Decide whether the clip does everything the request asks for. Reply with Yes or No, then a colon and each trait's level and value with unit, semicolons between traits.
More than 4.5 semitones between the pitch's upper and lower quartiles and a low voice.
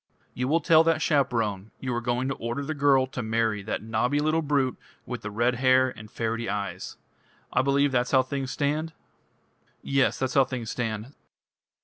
No: average, 3.4 semitones; low, 130 Hz